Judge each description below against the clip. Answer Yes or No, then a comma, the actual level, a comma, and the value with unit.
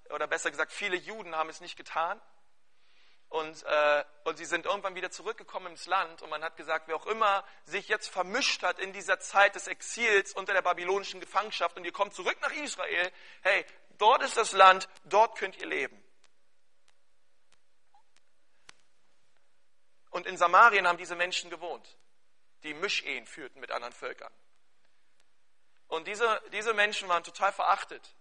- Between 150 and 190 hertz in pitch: Yes, medium, 185 Hz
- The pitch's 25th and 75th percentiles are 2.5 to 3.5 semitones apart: Yes, average, 3.0 semitones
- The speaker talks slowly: No, average, 155 wpm